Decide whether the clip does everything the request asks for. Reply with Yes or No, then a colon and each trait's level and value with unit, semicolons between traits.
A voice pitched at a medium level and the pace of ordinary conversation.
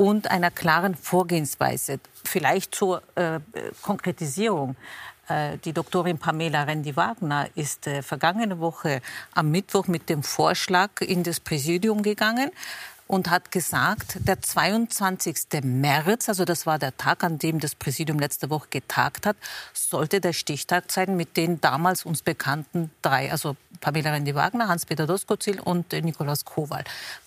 Yes: medium, 170 Hz; average, 140 wpm